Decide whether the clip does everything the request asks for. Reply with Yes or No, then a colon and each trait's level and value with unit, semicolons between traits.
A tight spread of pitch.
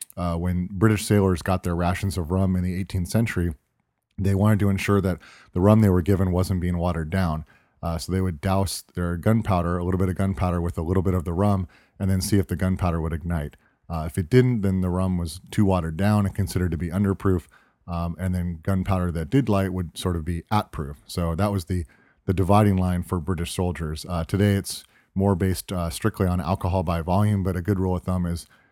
Yes: narrow, 2.0 semitones